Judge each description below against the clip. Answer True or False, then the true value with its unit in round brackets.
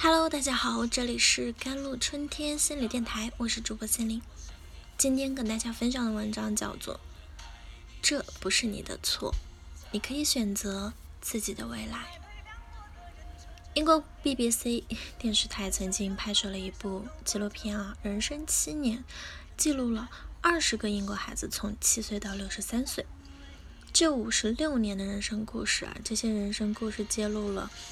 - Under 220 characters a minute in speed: False (245 characters per minute)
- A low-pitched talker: False (215 Hz)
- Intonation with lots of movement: False (3.6 semitones)